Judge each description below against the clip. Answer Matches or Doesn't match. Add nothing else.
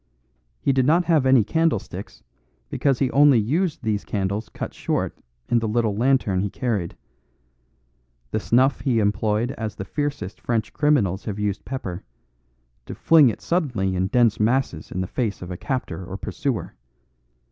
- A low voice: Matches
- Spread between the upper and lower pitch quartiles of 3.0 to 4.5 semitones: Doesn't match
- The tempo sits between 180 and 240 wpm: Doesn't match